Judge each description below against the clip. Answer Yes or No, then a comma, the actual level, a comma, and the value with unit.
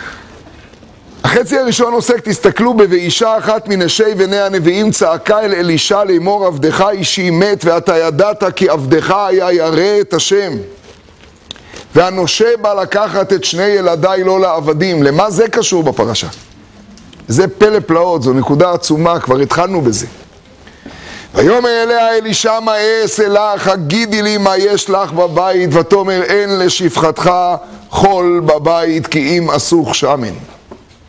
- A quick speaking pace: No, average, 130 wpm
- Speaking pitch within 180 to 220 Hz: Yes, high, 190 Hz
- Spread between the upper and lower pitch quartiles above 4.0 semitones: No, average, 3.7 semitones